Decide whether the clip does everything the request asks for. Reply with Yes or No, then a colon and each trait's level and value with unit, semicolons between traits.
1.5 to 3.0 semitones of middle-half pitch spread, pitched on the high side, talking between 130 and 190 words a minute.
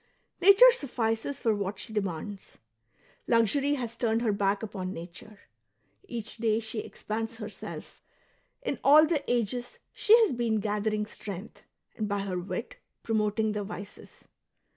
Yes: average, 2.7 semitones; high, 220 Hz; average, 140 wpm